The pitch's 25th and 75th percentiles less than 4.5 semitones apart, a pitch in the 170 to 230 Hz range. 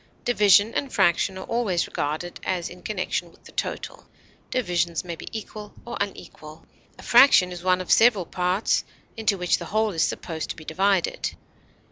Yes: average, 3.6 semitones; medium, 185 Hz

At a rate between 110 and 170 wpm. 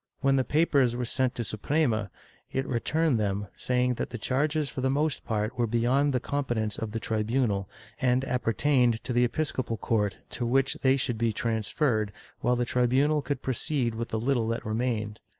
No: average, 185 wpm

